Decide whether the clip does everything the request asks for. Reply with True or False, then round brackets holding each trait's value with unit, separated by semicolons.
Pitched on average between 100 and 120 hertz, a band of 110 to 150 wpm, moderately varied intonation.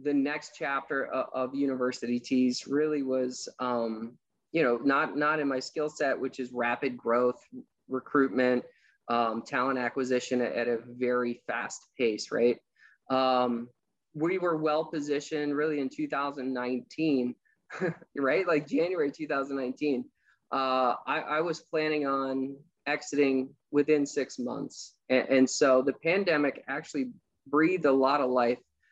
False (135 Hz; 145 wpm; 3.0 semitones)